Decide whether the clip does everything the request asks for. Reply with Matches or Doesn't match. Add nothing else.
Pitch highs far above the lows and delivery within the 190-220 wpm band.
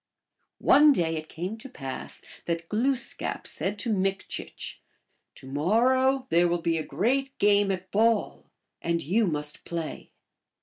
Doesn't match